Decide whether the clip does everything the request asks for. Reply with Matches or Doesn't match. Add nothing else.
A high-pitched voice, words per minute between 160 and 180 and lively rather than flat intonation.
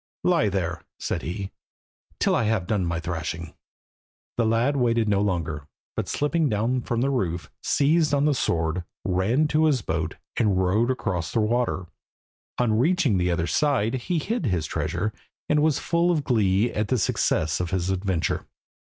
Doesn't match